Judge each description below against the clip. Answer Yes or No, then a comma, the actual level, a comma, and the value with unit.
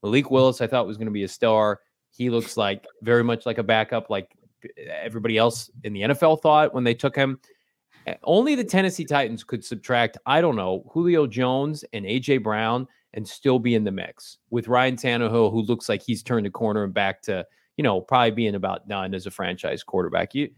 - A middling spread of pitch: Yes, average, 3.5 semitones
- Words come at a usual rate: No, fast, 215 wpm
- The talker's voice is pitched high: No, low, 120 Hz